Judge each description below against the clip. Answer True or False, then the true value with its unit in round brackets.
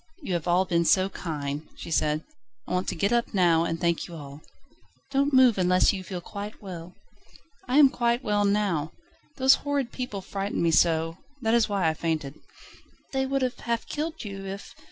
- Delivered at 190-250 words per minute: True (195 wpm)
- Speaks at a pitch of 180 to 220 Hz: True (190 Hz)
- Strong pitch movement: True (6.0 semitones)